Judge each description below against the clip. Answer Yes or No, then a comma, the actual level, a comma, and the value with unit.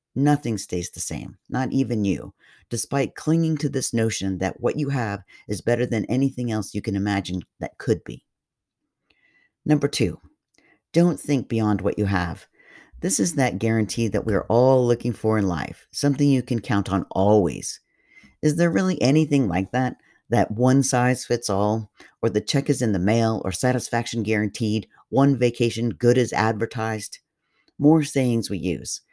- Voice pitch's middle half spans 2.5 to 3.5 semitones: No, average, 4.3 semitones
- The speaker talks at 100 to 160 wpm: No, average, 170 wpm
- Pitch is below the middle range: Yes, low, 115 Hz